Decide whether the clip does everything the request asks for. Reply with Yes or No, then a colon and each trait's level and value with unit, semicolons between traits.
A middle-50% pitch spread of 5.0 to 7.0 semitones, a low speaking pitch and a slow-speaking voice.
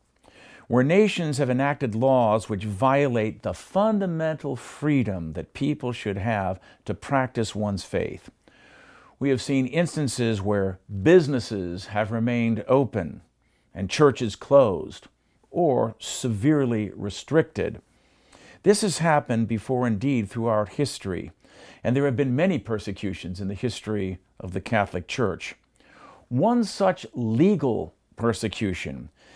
Yes: average, 5.3 semitones; low, 115 Hz; slow, 120 wpm